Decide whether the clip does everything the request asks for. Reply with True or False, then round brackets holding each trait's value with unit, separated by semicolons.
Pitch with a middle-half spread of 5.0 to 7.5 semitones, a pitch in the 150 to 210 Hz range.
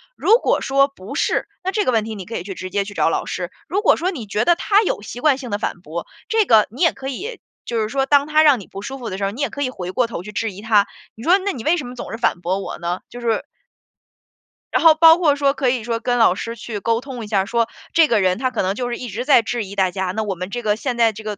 False (5.4 semitones; 230 Hz)